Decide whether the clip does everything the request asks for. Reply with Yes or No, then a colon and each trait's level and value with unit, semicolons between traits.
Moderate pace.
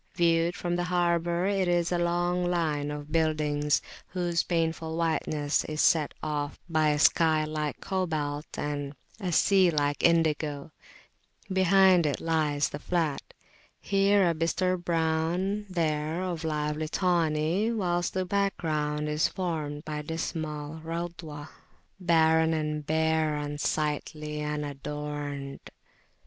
No: slow, 125 wpm